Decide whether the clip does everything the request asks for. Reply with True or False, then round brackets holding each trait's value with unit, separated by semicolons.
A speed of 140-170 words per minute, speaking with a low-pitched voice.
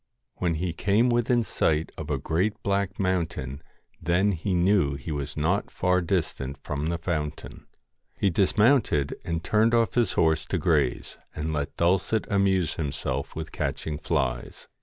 True (155 wpm; 85 Hz)